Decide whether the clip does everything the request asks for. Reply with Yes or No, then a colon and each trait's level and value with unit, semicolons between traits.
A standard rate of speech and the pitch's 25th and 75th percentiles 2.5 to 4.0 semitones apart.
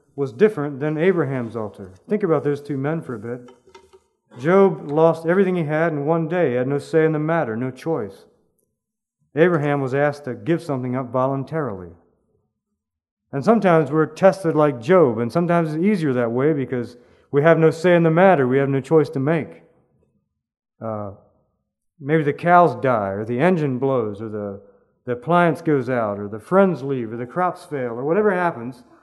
No: average, 185 wpm; average, 5.1 semitones